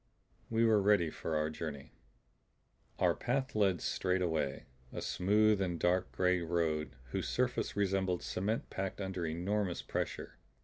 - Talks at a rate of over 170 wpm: No, average, 140 wpm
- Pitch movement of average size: Yes, average, 3.6 semitones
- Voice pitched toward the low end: Yes, very low, 90 Hz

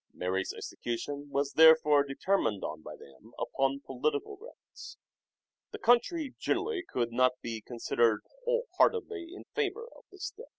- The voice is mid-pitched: Yes, medium, 150 Hz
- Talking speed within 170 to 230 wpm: No, average, 140 wpm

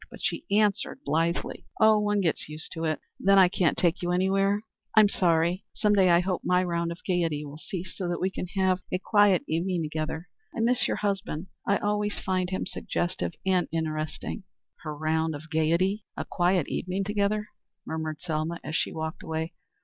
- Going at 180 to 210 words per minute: Yes, average, 190 wpm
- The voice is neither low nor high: Yes, medium, 180 Hz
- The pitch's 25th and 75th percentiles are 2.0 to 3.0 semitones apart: No, average, 3.4 semitones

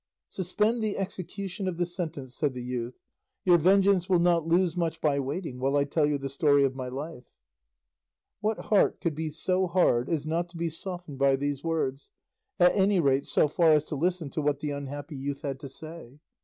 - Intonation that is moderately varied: Yes, average, 4.2 semitones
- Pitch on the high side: No, medium, 160 Hz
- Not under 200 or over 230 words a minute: Yes, fast, 205 wpm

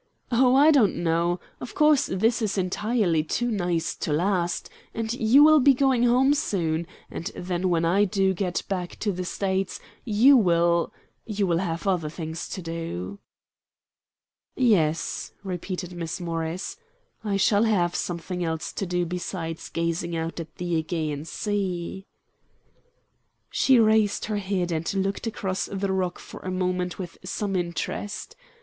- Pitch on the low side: No, medium, 185 Hz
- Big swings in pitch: No, average, 3.6 semitones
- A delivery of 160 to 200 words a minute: No, average, 150 wpm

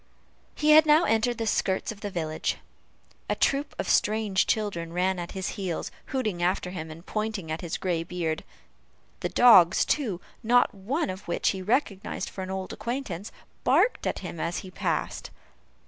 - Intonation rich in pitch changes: No, average, 4.4 semitones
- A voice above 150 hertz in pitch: Yes, high, 190 Hz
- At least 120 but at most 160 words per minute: No, average, 175 wpm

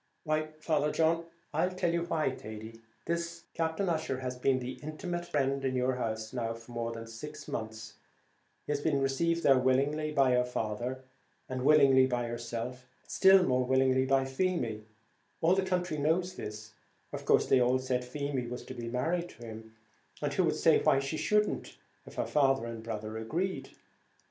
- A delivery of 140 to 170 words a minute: No, average, 185 wpm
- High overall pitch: No, low, 135 Hz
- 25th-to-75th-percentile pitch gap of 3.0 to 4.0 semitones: No, average, 4.7 semitones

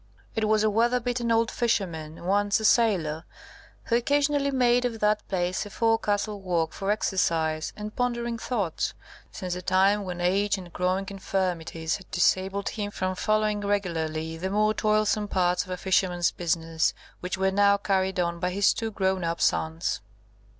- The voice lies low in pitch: No, high, 195 Hz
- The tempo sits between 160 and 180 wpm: Yes, average, 165 wpm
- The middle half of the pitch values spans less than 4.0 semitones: Yes, average, 3.2 semitones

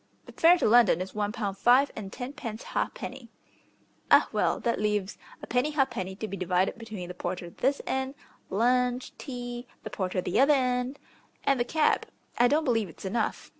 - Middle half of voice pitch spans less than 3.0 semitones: No, average, 4.9 semitones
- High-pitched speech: Yes, high, 235 Hz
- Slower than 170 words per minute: No, average, 180 wpm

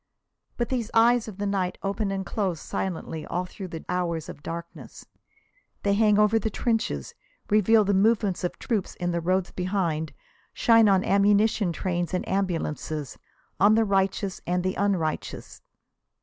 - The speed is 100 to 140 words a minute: No, average, 155 wpm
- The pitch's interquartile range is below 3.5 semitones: Yes, average, 3.1 semitones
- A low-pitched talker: No, high, 195 Hz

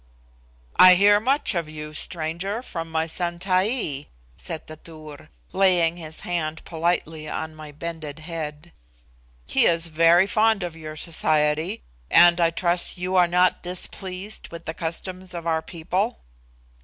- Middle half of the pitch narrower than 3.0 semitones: Yes, narrow, 2.6 semitones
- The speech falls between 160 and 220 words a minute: No, average, 145 wpm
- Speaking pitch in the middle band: Yes, medium, 170 Hz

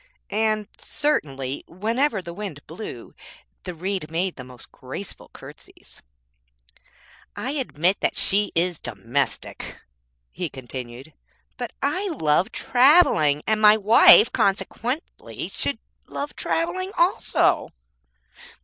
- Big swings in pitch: Yes, wide, 8.8 semitones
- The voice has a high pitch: Yes, high, 195 Hz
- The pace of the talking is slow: Yes, slow, 105 wpm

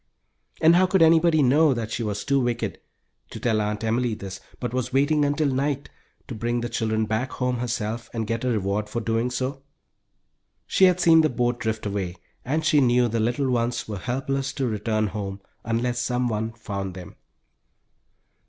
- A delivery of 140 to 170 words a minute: No, average, 180 wpm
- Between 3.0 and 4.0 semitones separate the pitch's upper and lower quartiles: Yes, average, 3.7 semitones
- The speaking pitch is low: Yes, low, 120 Hz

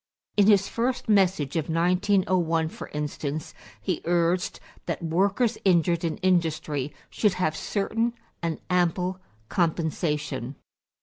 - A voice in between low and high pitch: Yes, medium, 175 Hz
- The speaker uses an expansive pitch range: No, average, 3.2 semitones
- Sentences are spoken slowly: Yes, slow, 115 wpm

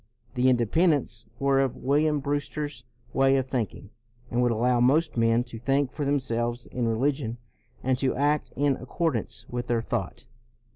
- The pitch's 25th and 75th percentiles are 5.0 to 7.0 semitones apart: No, average, 3.0 semitones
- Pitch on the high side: No, low, 130 Hz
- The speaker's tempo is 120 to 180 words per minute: Yes, average, 160 wpm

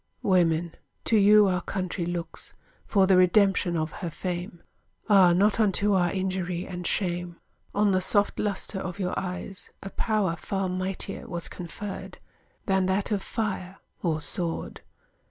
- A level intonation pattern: Yes, narrow, 2.0 semitones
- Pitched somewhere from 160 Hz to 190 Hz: Yes, medium, 185 Hz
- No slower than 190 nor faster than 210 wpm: No, average, 150 wpm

